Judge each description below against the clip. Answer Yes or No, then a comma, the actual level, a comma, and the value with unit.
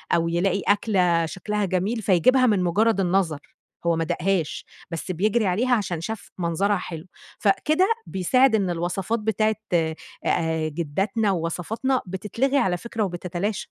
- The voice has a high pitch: Yes, high, 195 Hz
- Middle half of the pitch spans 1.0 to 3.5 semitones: No, average, 4.0 semitones